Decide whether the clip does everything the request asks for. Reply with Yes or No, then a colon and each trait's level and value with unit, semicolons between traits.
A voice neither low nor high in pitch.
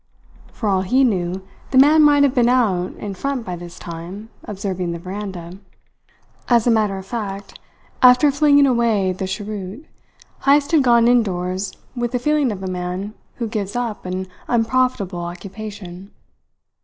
No: high, 210 Hz